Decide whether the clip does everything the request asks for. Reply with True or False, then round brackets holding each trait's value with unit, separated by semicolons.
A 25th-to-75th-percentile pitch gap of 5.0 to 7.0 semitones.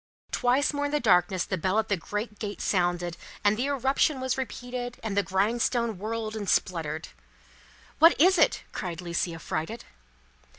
True (5.4 semitones)